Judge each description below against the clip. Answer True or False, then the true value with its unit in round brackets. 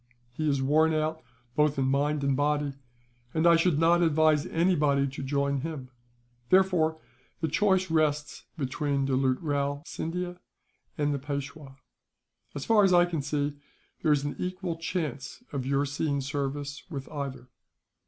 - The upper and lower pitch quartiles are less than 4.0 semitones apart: True (2.6 semitones)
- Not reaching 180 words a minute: True (155 wpm)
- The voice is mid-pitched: True (145 Hz)